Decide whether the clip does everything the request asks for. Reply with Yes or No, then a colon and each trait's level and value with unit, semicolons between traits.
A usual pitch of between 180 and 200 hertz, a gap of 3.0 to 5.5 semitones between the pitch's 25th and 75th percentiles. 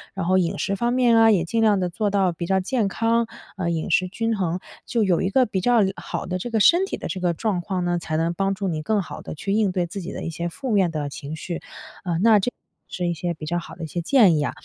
Yes: medium, 185 Hz; average, 4.1 semitones